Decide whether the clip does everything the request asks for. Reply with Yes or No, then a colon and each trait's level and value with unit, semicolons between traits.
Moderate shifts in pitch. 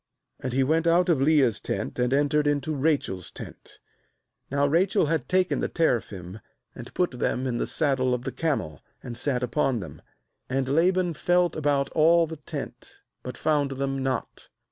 Yes: average, 4.1 semitones